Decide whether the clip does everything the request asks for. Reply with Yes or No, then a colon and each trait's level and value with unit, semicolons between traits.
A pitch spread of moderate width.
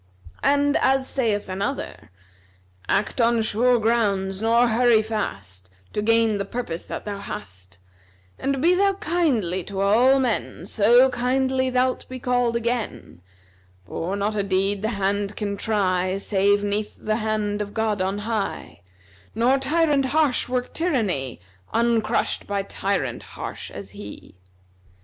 Yes: average, 4.2 semitones